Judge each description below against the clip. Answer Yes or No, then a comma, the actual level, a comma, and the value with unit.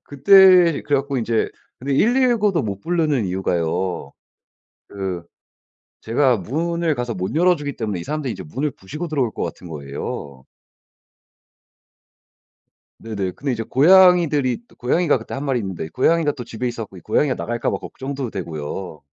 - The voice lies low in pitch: Yes, low, 130 Hz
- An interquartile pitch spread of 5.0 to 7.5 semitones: No, wide, 7.9 semitones